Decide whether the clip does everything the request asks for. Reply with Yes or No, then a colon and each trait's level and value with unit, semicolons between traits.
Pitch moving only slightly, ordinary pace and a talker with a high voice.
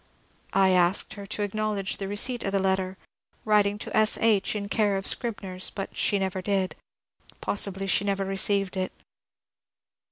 Yes: narrow, 1.4 semitones; average, 160 wpm; high, 195 Hz